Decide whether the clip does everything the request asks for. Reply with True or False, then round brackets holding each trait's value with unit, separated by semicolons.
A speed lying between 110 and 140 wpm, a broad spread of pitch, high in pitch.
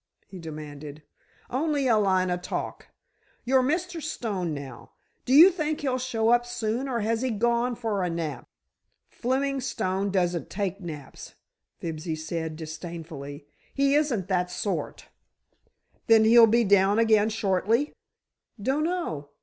True (135 wpm; 6.7 semitones; 215 Hz)